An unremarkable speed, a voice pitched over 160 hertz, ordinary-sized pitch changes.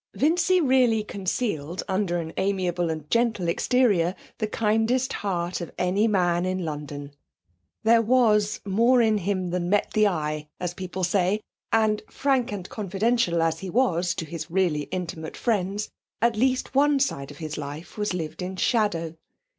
Yes: average, 160 wpm; high, 190 Hz; average, 4.7 semitones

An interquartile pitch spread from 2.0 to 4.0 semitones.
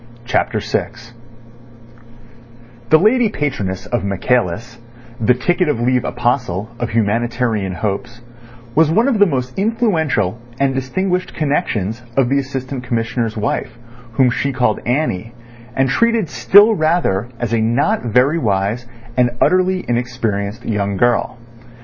No: average, 5.1 semitones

